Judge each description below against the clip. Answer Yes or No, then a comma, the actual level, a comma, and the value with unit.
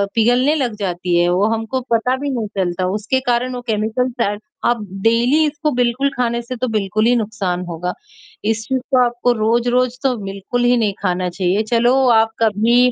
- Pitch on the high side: Yes, high, 230 Hz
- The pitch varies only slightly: No, average, 3.3 semitones